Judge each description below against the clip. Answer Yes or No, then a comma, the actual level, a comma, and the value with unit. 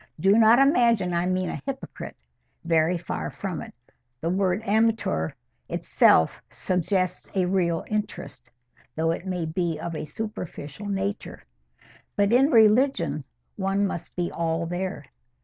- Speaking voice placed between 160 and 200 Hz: Yes, medium, 185 Hz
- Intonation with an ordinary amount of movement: Yes, average, 4.0 semitones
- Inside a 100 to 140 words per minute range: Yes, slow, 135 wpm